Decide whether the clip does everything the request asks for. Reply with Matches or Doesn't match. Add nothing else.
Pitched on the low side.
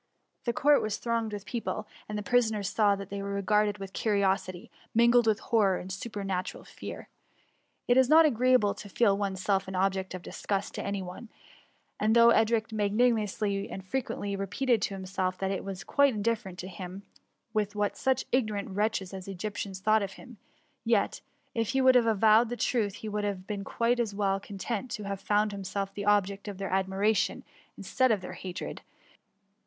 Doesn't match